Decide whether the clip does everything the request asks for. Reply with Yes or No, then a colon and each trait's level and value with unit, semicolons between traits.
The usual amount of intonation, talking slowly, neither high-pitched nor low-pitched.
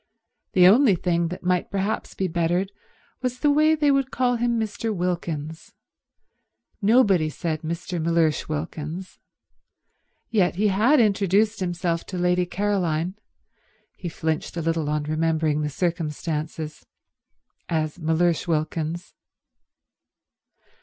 Yes: average, 4.0 semitones; slow, 110 wpm; medium, 175 Hz